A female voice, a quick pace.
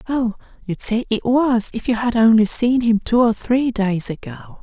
No: male; fast, 210 wpm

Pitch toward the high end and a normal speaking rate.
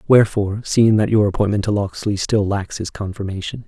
No: low, 100 Hz; average, 180 wpm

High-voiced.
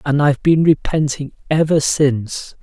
No: medium, 145 Hz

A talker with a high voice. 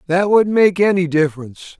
No: medium, 180 Hz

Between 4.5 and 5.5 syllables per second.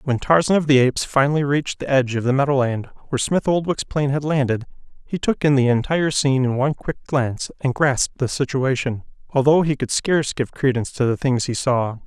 No: 6.0 syllables/s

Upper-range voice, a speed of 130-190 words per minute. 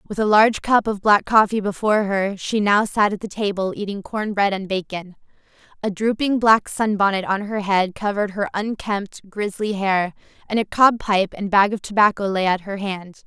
No: high, 205 Hz; average, 200 wpm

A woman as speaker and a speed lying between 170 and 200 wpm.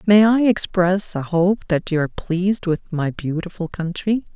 Yes: female; average, 180 wpm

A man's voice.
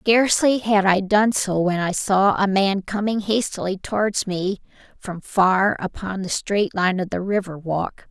No: female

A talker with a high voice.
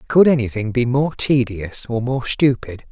No: low, 125 Hz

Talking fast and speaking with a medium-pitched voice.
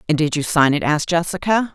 Yes: fast, 240 wpm; medium, 160 Hz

